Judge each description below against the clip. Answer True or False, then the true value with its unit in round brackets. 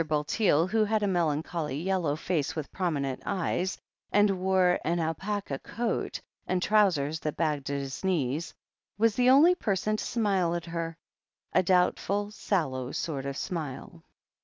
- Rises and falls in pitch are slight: False (4.8 semitones)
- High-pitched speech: False (175 Hz)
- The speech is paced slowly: False (155 wpm)